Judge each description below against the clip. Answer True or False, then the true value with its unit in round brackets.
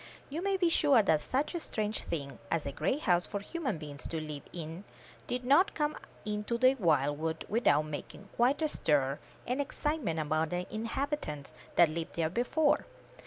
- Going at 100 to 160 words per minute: False (180 wpm)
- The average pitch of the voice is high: True (200 Hz)